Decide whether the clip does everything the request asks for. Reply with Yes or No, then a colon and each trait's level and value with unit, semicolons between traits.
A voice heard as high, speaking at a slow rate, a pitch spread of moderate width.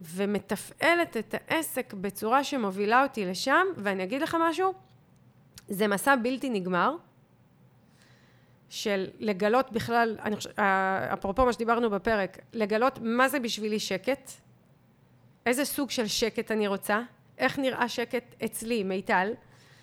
No: high, 225 Hz; average, 120 wpm; average, 4.3 semitones